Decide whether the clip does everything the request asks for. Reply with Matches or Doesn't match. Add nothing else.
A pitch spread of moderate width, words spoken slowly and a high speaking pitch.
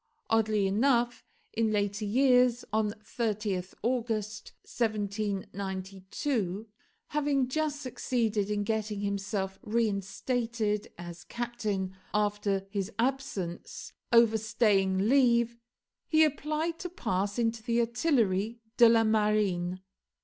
Matches